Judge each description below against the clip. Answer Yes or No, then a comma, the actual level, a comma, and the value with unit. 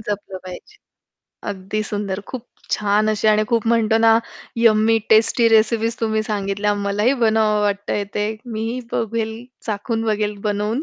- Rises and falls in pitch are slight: Yes, narrow, 1.5 semitones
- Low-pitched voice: No, high, 215 Hz